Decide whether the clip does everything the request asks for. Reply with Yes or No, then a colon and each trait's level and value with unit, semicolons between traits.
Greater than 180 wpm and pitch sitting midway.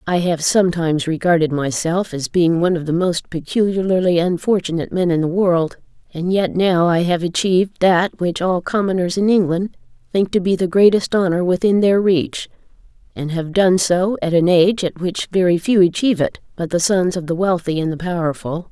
Yes: average, 190 wpm; medium, 175 Hz